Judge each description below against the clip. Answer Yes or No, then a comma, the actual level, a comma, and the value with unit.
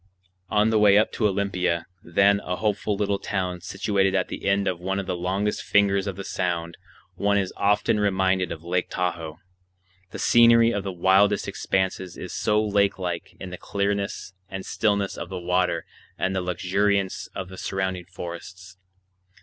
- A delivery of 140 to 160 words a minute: No, average, 175 wpm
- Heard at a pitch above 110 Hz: No, very low, 95 Hz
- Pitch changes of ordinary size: No, narrow, 1.8 semitones